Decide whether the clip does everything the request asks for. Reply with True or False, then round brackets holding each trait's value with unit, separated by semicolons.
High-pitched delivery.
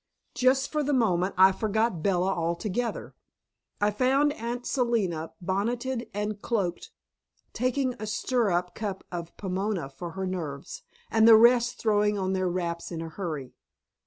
True (205 Hz)